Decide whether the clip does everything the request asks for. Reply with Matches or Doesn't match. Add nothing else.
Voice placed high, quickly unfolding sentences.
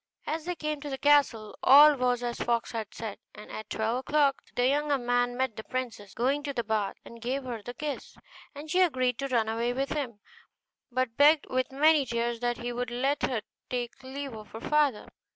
Matches